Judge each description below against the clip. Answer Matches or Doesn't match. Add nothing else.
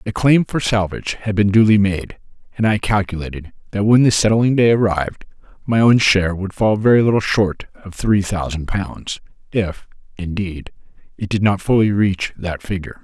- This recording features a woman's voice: Doesn't match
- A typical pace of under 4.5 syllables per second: Doesn't match